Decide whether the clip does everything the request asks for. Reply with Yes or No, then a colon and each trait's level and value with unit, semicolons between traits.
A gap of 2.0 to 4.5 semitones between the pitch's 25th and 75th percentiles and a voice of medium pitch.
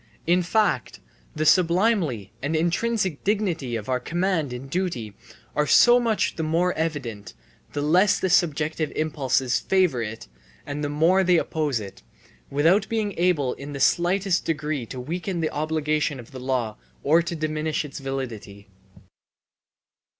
No: average, 4.9 semitones; medium, 155 Hz